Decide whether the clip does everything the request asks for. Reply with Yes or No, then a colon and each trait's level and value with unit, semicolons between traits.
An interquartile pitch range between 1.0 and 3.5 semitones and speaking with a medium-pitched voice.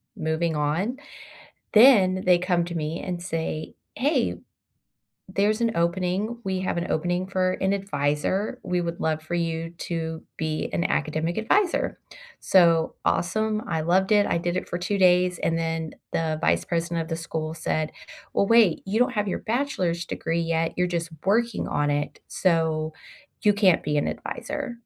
Yes: average, 3.2 semitones; medium, 175 Hz